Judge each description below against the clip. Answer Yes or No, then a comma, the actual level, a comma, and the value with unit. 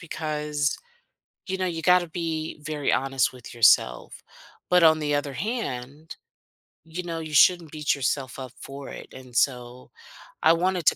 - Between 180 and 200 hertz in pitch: No, medium, 150 Hz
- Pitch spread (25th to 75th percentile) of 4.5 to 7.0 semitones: No, average, 3.8 semitones